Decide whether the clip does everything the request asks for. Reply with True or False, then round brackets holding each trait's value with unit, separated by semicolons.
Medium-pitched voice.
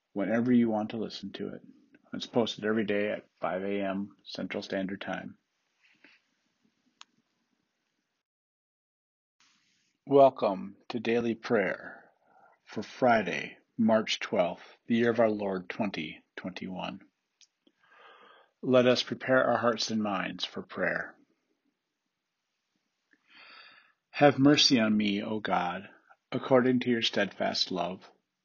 False (115 Hz)